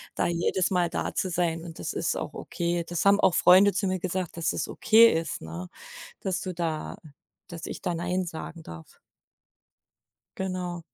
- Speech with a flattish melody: Yes, narrow, 2.0 semitones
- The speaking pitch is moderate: Yes, medium, 175 Hz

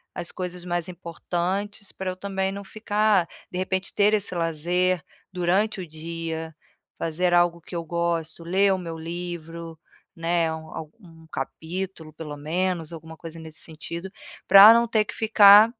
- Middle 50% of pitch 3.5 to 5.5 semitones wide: No, average, 2.7 semitones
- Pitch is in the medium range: Yes, medium, 175 Hz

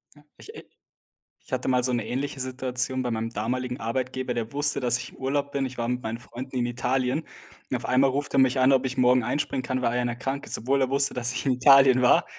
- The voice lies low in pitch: Yes, low, 130 Hz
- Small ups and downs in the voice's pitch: Yes, narrow, 1.5 semitones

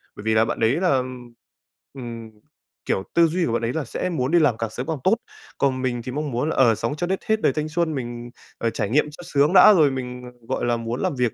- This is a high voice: No, low, 130 Hz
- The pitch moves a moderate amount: Yes, average, 4.8 semitones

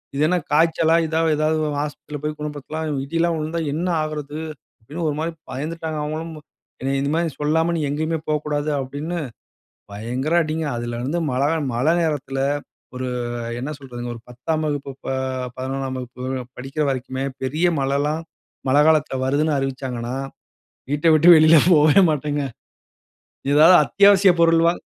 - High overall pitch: No, medium, 150 Hz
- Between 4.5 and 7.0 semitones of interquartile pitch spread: No, average, 3.1 semitones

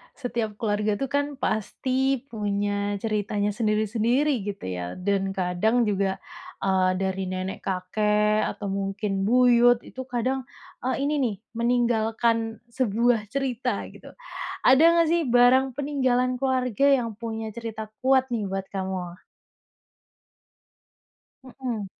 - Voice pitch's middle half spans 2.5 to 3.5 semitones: No, average, 3.9 semitones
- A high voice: Yes, high, 225 Hz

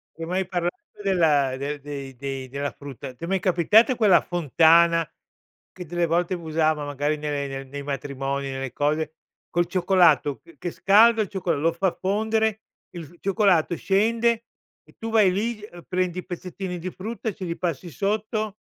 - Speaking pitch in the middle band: Yes, medium, 175 Hz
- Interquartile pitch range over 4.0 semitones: Yes, average, 5.0 semitones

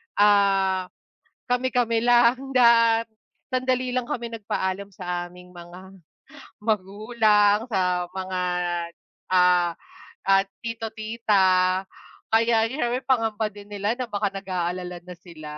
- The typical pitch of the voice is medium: No, high, 205 Hz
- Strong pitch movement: No, average, 3.9 semitones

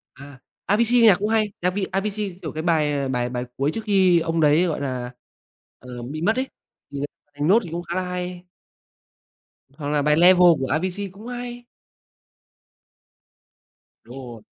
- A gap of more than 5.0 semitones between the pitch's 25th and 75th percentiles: Yes, wide, 5.6 semitones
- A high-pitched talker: No, medium, 170 Hz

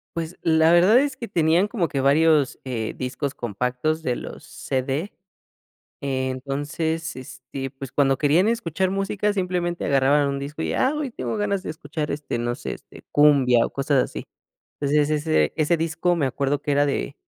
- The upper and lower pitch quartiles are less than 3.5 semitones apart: No, average, 4.0 semitones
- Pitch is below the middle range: No, medium, 150 Hz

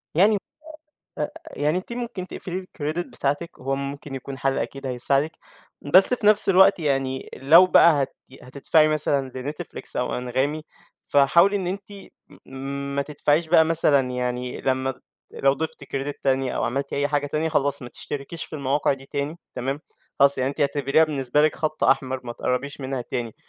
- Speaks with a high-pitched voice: No, medium, 140 Hz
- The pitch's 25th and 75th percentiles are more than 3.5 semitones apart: No, average, 3.0 semitones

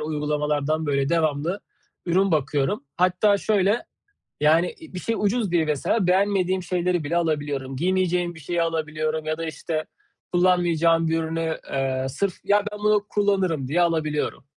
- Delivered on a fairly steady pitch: No, average, 3.3 semitones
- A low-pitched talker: No, medium, 165 Hz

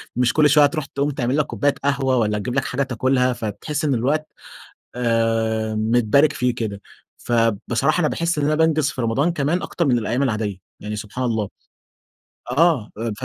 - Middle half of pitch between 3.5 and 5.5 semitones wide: Yes, average, 4.3 semitones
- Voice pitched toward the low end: Yes, low, 125 Hz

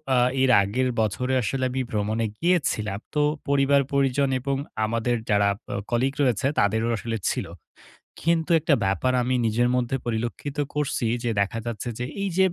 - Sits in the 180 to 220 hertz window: No, low, 125 Hz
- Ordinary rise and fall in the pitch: Yes, average, 3.7 semitones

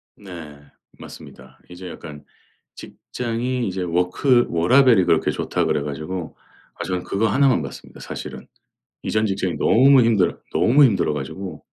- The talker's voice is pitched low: Yes, very low, 95 Hz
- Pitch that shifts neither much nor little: No, wide, 6.0 semitones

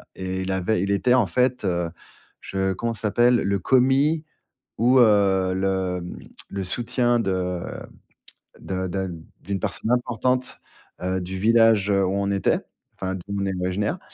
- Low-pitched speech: Yes, low, 100 Hz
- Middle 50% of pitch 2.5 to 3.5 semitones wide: No, average, 4.0 semitones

